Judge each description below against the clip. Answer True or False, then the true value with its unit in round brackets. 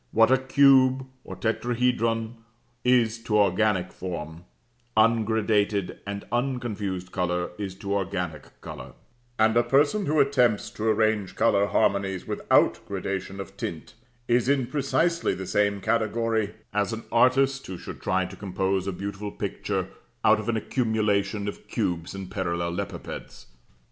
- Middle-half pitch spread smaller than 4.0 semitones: True (3.5 semitones)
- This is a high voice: False (105 Hz)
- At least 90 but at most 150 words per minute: True (140 wpm)